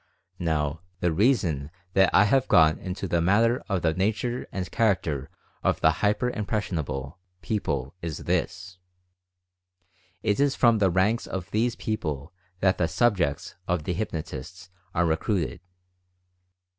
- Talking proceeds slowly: No, average, 145 wpm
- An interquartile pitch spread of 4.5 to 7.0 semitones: Yes, average, 4.8 semitones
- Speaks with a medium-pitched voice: No, very low, 90 Hz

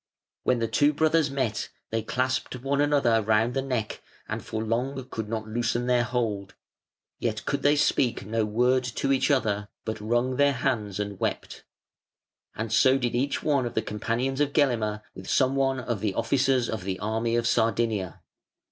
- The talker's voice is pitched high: No, low, 120 Hz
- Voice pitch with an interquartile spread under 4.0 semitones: Yes, average, 3.4 semitones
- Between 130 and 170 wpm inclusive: No, average, 180 wpm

